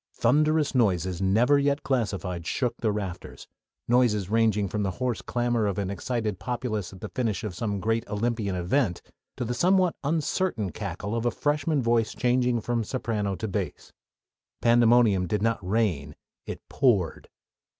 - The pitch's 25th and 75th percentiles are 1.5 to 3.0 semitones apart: No, average, 3.8 semitones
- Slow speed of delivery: No, average, 155 wpm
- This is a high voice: No, low, 115 Hz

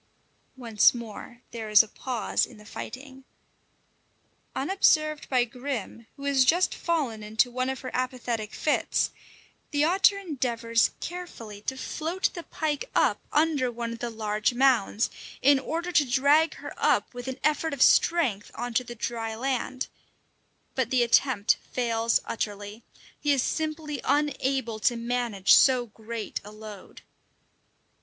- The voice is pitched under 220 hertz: No, very high, 250 Hz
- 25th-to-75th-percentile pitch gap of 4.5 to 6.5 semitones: No, average, 4.0 semitones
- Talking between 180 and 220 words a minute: No, average, 145 wpm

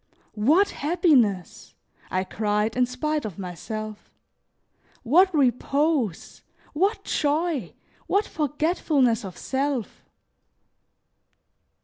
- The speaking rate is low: Yes, slow, 80 wpm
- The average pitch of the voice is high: Yes, very high, 270 Hz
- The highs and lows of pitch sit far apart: Yes, wide, 6.5 semitones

